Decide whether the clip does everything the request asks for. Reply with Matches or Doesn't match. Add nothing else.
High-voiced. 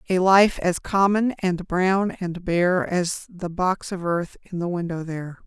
Doesn't match